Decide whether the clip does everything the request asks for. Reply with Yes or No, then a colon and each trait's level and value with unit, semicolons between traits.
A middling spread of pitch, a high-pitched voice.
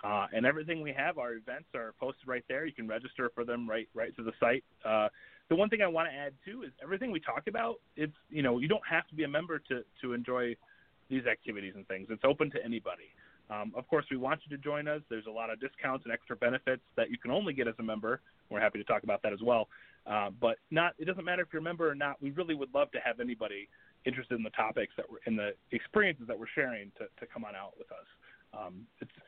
No: average, 4.8 semitones; low, 130 Hz